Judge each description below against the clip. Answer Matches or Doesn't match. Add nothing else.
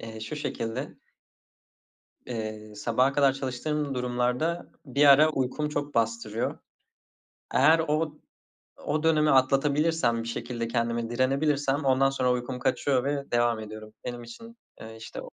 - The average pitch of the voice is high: Doesn't match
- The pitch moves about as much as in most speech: Matches